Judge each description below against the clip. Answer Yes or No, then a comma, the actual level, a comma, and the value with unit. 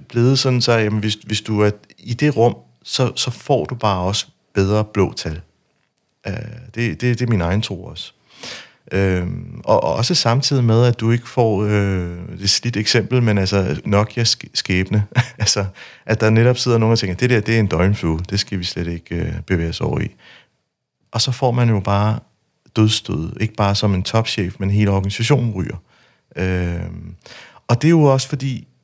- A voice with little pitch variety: No, average, 3.6 semitones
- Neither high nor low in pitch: No, low, 105 Hz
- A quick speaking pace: No, average, 195 wpm